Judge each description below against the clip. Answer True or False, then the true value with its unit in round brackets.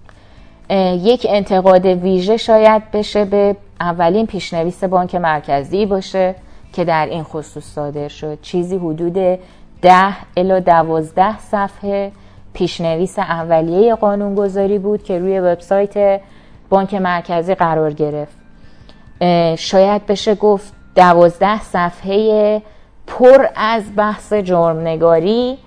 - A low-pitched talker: False (185 Hz)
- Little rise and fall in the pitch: False (3.3 semitones)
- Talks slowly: True (100 wpm)